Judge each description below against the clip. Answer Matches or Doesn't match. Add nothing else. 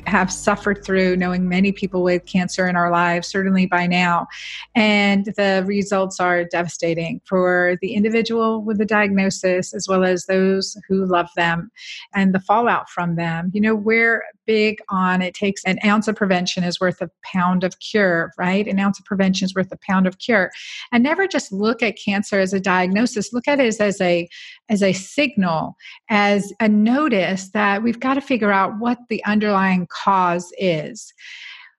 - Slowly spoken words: Doesn't match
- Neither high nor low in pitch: Doesn't match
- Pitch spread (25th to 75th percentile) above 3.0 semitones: Doesn't match